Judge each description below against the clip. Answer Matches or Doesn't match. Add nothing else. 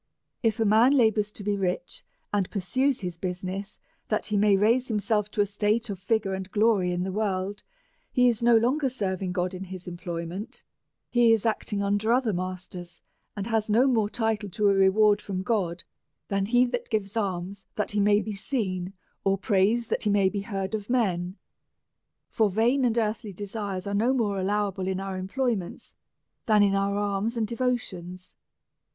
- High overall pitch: Matches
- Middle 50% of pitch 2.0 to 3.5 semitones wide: Matches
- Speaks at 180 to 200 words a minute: Matches